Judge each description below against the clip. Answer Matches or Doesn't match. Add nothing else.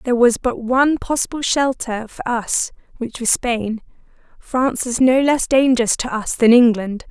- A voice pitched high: Matches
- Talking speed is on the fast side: Doesn't match